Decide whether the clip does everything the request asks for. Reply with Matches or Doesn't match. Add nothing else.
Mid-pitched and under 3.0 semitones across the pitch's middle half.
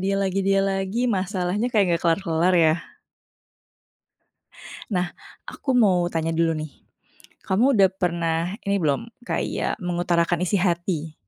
Matches